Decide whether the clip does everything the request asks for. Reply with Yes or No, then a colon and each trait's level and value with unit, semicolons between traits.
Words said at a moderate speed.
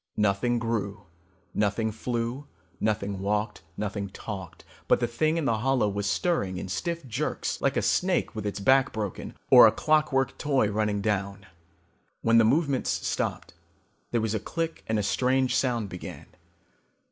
Yes: average, 160 wpm